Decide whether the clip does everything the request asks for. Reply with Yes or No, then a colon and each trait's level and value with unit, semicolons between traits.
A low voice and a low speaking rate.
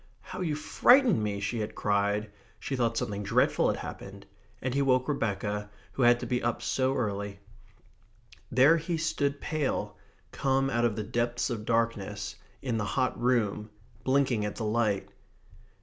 No: low, 120 Hz; average, 165 wpm